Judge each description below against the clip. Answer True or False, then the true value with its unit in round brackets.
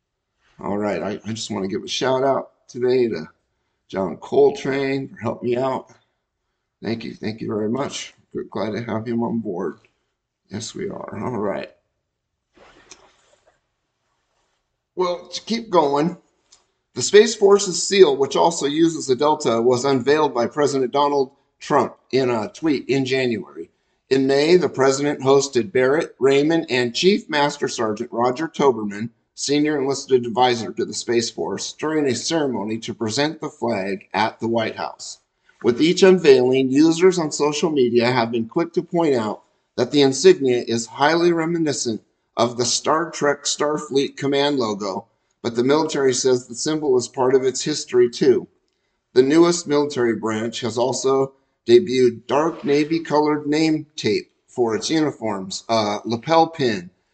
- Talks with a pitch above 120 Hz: True (140 Hz)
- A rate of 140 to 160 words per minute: True (155 wpm)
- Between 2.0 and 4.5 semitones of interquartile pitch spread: False (5.1 semitones)